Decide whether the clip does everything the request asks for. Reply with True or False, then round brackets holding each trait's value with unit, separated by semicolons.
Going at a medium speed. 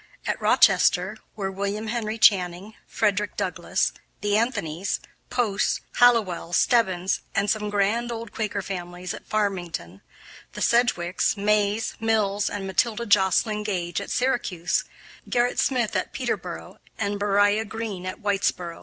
False (125 wpm)